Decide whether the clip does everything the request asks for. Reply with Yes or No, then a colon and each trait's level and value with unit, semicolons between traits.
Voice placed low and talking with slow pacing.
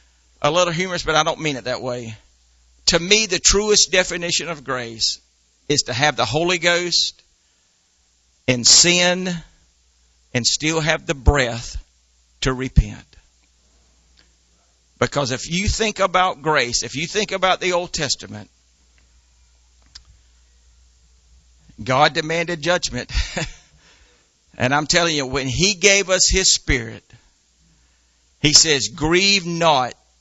Yes: low, 120 Hz; slow, 125 wpm